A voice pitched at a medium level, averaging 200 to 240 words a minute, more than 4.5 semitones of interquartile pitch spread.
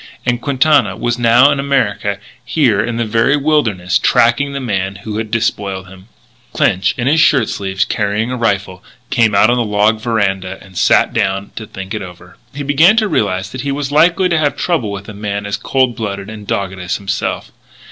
No: low, 110 Hz; fast, 205 wpm; average, 5.2 semitones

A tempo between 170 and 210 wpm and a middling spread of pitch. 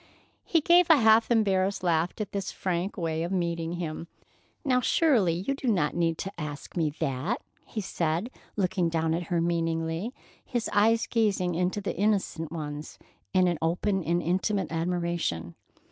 No: average, 160 wpm; average, 3.9 semitones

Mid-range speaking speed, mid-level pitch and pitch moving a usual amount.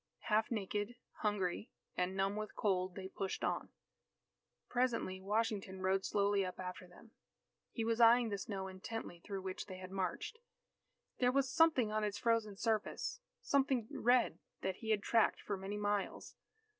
No: average, 155 wpm; high, 205 Hz; average, 3.1 semitones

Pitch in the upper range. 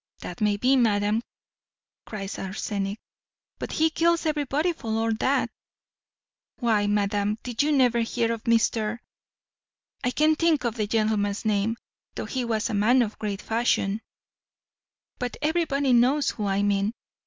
Yes: high, 225 Hz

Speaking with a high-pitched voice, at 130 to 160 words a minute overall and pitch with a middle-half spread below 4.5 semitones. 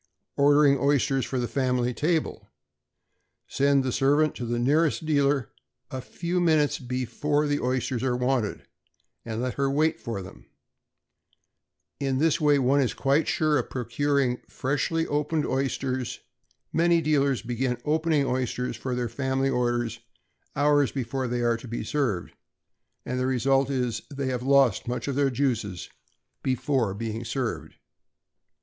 No: low, 135 Hz; average, 145 wpm; average, 2.8 semitones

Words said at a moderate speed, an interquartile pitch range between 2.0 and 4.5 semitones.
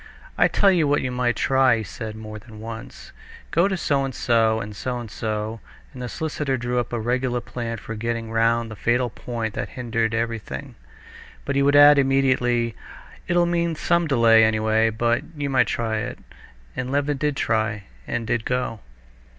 Yes: average, 185 wpm; average, 3.3 semitones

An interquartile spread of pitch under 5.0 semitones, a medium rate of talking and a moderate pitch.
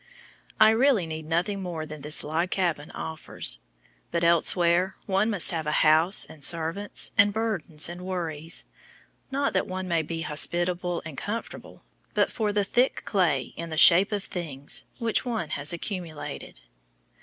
Yes: average, 3.9 semitones; average, 155 wpm; medium, 175 Hz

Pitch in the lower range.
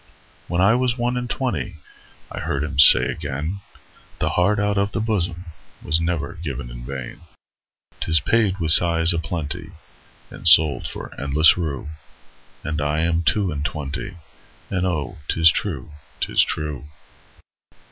Yes: very low, 80 Hz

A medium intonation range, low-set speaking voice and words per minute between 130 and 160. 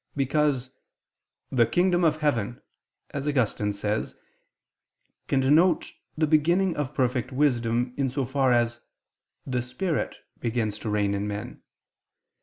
Yes: average, 4.1 semitones; low, 130 Hz; slow, 135 wpm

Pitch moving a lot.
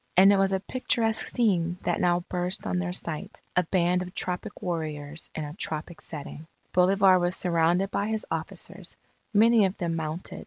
No: average, 2.7 semitones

